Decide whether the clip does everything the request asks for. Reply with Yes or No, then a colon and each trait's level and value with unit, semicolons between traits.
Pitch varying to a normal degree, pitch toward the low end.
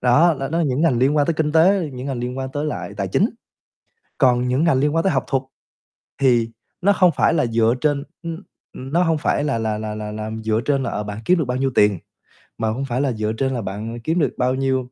Yes: average, 4.8 semitones; low, 130 Hz